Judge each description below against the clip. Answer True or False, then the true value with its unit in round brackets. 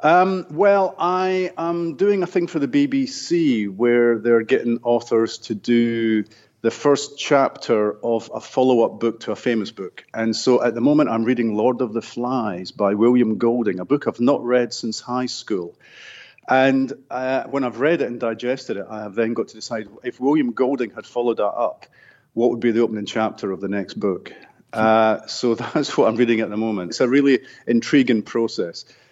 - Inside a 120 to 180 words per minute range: False (200 wpm)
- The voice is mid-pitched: False (120 Hz)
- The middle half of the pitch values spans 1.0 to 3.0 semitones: False (3.7 semitones)